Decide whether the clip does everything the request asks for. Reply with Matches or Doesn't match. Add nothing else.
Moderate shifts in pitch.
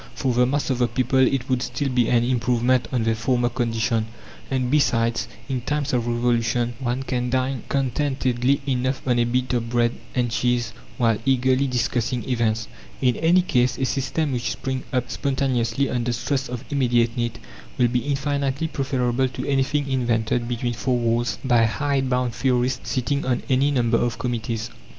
Doesn't match